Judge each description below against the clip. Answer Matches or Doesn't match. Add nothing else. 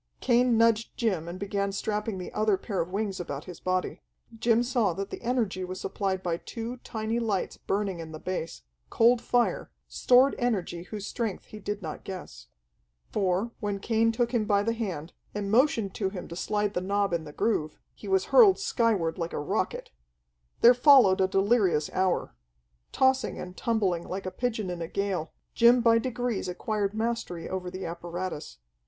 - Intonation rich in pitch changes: Doesn't match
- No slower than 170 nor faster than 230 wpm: Matches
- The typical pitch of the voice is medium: Doesn't match